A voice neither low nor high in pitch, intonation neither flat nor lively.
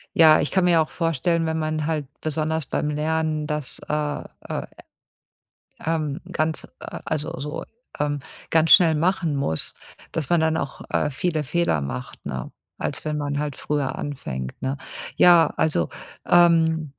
No: medium, 155 Hz; narrow, 1.9 semitones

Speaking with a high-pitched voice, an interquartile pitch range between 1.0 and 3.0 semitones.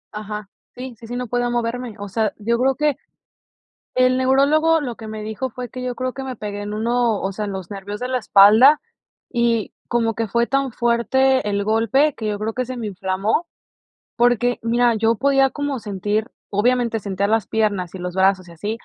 No: high, 230 Hz; average, 3.4 semitones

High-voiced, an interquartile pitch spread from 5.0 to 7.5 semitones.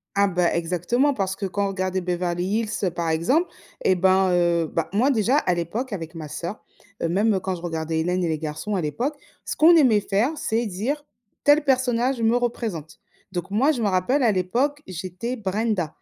Yes: high, 195 Hz; wide, 5.4 semitones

